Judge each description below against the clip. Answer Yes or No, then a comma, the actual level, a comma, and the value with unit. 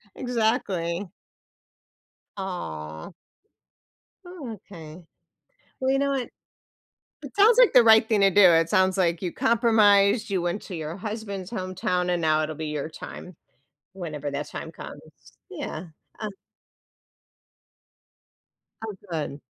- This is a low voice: No, high, 190 Hz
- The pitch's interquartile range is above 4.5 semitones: Yes, average, 5.1 semitones